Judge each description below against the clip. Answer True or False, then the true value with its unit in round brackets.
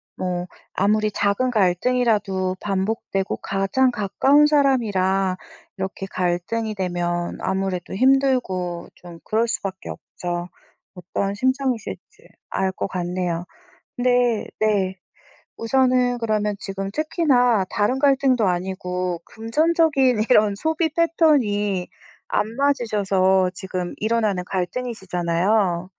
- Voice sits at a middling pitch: False (205 Hz)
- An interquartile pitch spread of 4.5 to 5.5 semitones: True (5.2 semitones)